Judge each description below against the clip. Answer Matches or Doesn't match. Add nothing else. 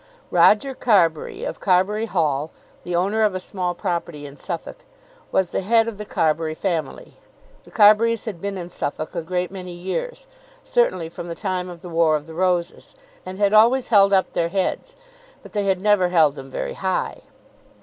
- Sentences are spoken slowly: Doesn't match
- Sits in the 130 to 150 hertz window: Doesn't match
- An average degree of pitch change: Matches